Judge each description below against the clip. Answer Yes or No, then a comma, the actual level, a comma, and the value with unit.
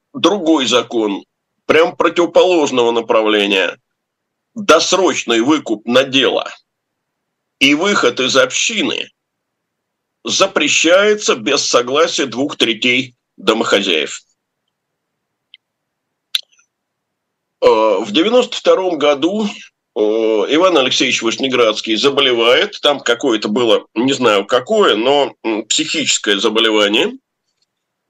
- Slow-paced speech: Yes, slow, 75 wpm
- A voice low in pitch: No, medium, 170 Hz